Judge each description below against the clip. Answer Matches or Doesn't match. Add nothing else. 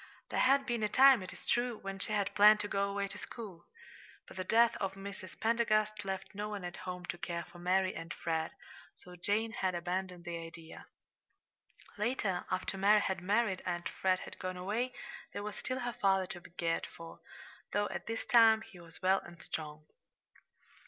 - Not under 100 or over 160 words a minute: Doesn't match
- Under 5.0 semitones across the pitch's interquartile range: Matches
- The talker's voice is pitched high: Matches